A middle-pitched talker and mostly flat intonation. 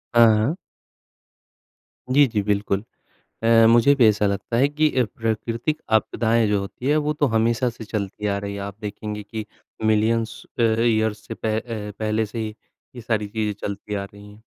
No: low, 110 Hz; narrow, 2.0 semitones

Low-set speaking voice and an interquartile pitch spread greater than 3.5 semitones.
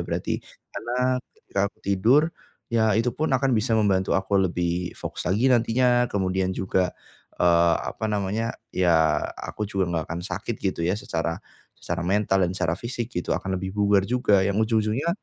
Yes: low, 100 Hz; average, 3.9 semitones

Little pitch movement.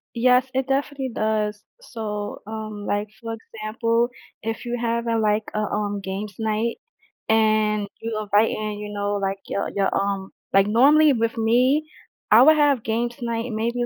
Yes: narrow, 2.2 semitones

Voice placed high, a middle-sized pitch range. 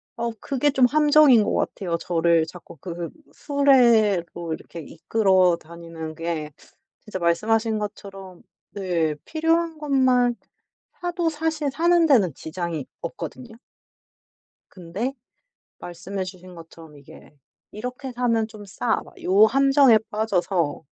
No: high, 210 Hz; wide, 7.4 semitones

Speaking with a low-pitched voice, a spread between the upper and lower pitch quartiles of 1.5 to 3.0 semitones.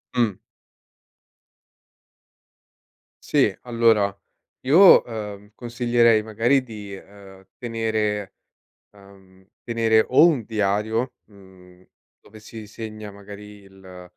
Yes: low, 105 Hz; narrow, 2.6 semitones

